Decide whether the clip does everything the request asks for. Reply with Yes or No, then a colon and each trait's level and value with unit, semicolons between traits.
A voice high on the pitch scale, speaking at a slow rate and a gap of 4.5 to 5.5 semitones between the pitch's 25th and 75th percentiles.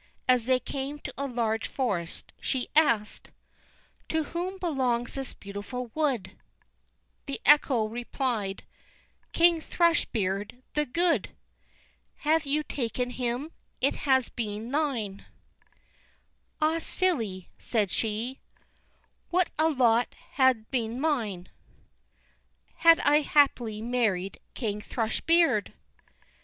Yes: very high, 250 Hz; slow, 110 wpm; average, 5.1 semitones